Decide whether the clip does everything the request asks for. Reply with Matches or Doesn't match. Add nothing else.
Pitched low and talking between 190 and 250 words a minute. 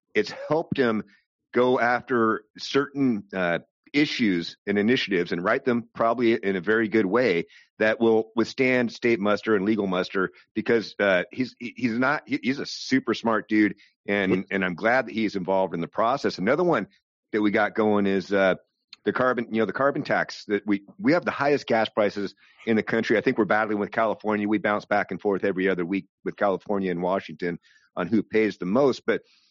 Matches